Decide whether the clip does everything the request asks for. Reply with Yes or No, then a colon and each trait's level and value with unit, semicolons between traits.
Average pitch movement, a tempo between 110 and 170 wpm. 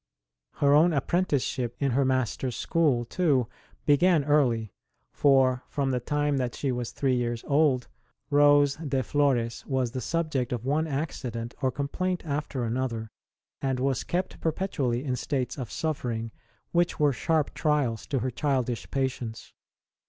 Yes: average, 3.1 semitones; average, 150 wpm